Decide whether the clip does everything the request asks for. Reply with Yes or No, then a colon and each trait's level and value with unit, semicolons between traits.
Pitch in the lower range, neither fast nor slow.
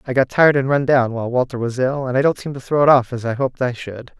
No: low, 130 Hz; fast, 330 wpm